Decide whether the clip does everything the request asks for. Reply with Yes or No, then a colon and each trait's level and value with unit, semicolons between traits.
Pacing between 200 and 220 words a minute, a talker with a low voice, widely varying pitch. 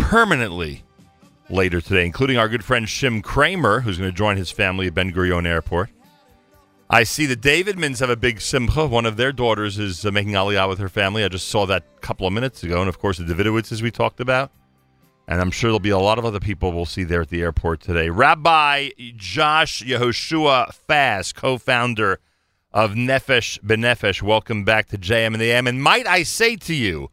No: fast, 205 wpm; low, 110 Hz; average, 4.8 semitones